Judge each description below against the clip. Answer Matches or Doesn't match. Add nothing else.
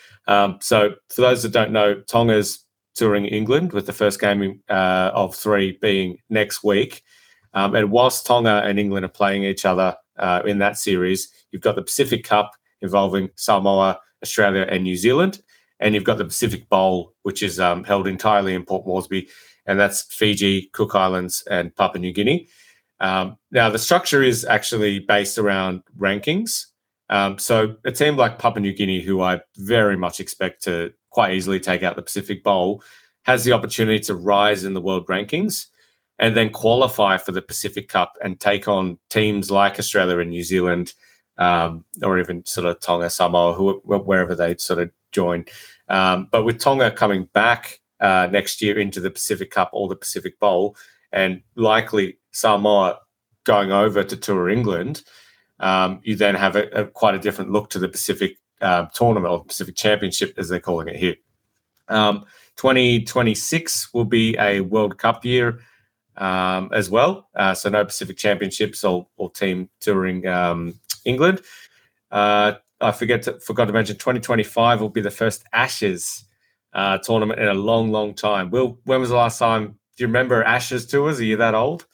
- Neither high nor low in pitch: Doesn't match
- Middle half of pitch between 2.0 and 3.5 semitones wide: Matches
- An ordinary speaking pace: Matches